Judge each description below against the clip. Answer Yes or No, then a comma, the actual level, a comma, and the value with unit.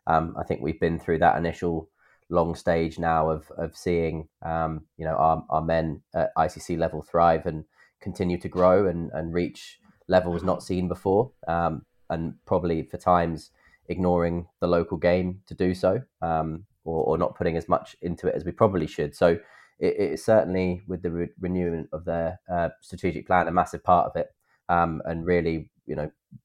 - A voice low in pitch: Yes, very low, 85 Hz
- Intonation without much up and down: Yes, narrow, 1.9 semitones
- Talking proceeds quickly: No, average, 190 wpm